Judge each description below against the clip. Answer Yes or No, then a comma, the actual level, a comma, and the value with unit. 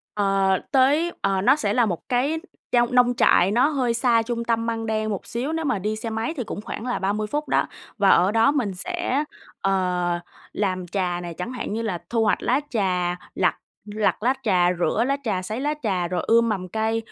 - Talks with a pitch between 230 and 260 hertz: No, high, 220 Hz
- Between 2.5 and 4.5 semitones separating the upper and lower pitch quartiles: Yes, average, 4.2 semitones